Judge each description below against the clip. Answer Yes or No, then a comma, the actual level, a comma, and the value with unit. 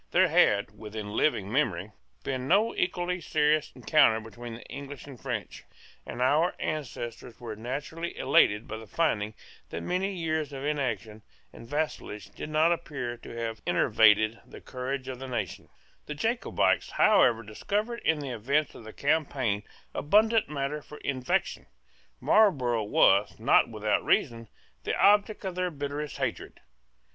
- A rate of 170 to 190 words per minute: No, average, 145 wpm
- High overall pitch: No, low, 135 Hz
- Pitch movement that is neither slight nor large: No, wide, 5.7 semitones